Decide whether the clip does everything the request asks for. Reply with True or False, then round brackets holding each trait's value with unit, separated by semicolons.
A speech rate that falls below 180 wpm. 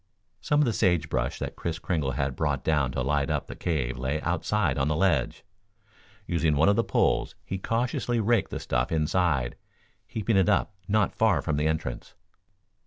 False (185 wpm)